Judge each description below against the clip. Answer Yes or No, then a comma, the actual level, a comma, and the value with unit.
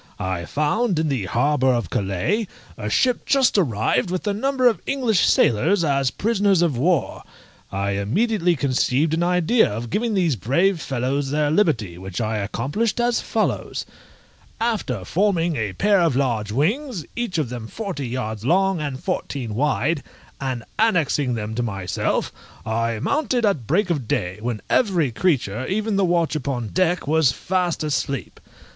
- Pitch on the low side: No, medium, 150 Hz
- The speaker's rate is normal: Yes, average, 160 wpm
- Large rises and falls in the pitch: Yes, wide, 8.5 semitones